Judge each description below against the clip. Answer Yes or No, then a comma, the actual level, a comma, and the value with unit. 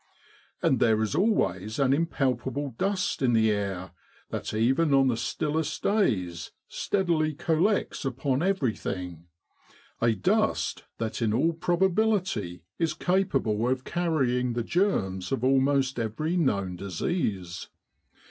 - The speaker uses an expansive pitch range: Yes, wide, 7.4 semitones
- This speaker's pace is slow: Yes, slow, 120 wpm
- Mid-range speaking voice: No, low, 130 Hz